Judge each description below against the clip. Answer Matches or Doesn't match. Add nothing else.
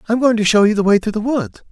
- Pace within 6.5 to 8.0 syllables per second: Matches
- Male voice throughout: Matches